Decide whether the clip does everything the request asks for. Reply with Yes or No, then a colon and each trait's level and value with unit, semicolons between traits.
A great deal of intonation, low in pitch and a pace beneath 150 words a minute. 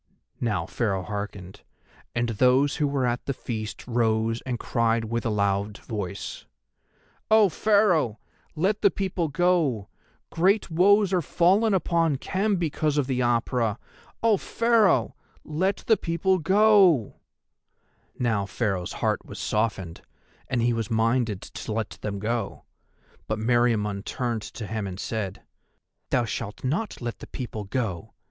Yes: wide, 7.9 semitones; low, 120 Hz; average, 140 wpm